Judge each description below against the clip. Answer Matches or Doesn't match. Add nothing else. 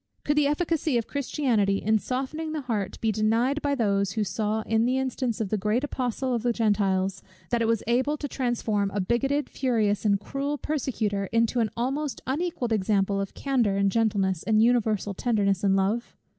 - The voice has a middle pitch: Doesn't match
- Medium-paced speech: Matches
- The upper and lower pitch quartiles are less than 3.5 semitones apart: Doesn't match